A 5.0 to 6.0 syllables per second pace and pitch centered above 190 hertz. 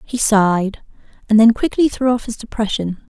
Yes: 5.1 syllables/s; high, 220 Hz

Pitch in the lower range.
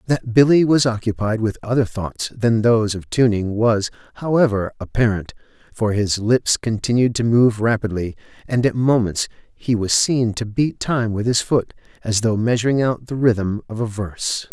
Yes: low, 115 Hz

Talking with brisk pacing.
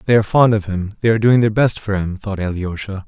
Yes: fast, 275 wpm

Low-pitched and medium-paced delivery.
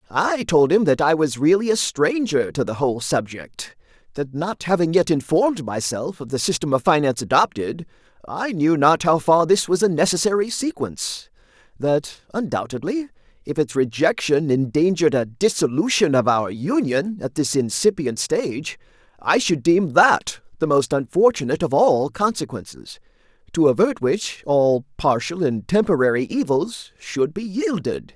No: medium, 160 Hz; average, 150 wpm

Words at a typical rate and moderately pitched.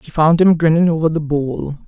No: fast, 225 wpm; medium, 155 Hz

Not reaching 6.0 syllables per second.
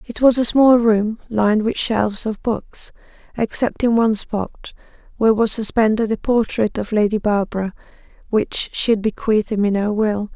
Yes: 5.0 syllables/s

